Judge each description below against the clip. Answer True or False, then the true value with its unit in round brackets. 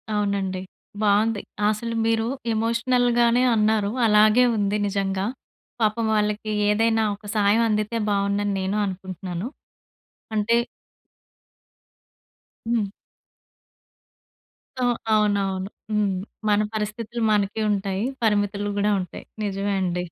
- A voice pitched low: False (210 Hz)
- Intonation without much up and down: True (1.8 semitones)